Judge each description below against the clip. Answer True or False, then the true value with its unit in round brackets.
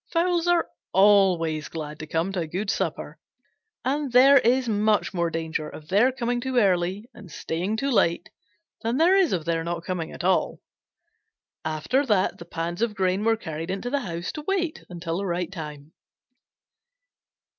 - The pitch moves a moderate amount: False (6.6 semitones)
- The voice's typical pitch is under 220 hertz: True (190 Hz)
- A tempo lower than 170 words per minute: False (175 wpm)